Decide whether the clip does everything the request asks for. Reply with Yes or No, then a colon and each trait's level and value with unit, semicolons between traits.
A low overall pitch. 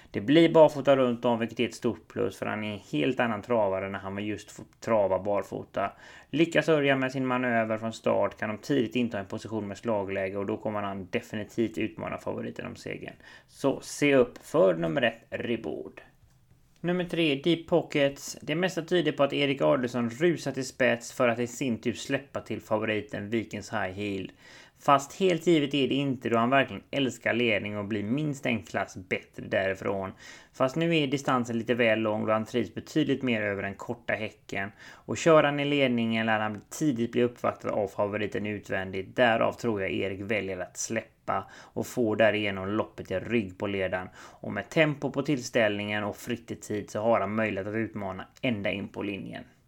Yes: low, 115 Hz